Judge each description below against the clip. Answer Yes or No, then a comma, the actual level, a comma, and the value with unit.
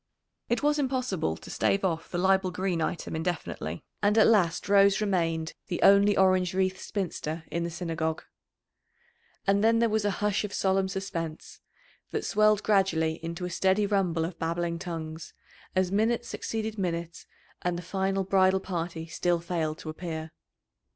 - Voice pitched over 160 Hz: Yes, medium, 185 Hz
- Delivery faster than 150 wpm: Yes, average, 160 wpm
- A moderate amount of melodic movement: Yes, average, 3.1 semitones